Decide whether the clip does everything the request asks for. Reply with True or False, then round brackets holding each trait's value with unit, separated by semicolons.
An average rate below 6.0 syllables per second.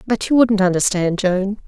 True (4.7 syllables/s)